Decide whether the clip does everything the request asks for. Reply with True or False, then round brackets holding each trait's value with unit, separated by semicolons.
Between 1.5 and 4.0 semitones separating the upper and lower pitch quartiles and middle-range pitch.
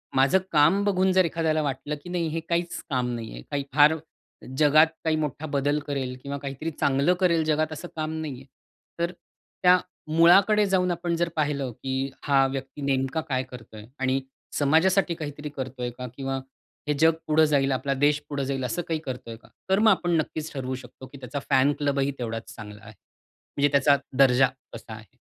True (3.4 semitones; 145 Hz)